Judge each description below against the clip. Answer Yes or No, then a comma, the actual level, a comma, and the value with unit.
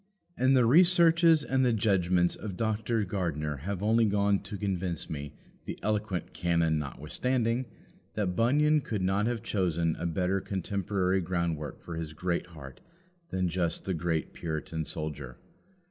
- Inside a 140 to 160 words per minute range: Yes, average, 145 wpm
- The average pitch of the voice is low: Yes, very low, 95 Hz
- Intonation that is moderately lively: Yes, average, 4.9 semitones